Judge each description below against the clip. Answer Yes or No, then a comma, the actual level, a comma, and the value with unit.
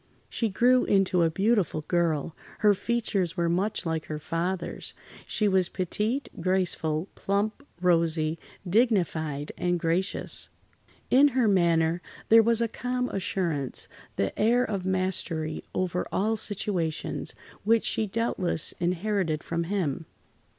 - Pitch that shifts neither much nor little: Yes, average, 4.3 semitones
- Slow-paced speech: Yes, slow, 120 wpm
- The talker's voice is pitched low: No, medium, 185 Hz